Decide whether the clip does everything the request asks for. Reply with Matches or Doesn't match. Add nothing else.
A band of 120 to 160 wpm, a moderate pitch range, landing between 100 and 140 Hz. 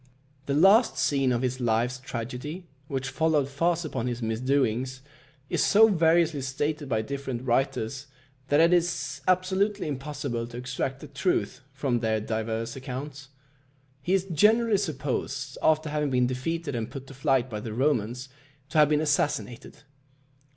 Matches